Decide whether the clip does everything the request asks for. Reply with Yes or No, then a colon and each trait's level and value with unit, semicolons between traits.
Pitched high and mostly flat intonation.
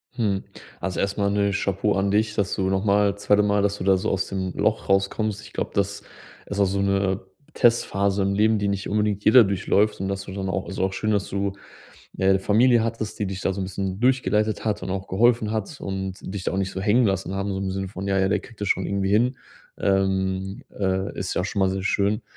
No: low, 100 Hz; narrow, 1.4 semitones